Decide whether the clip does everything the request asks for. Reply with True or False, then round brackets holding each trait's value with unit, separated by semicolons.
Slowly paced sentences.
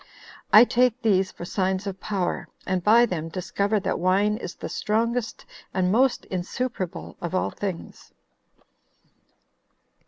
True (130 wpm)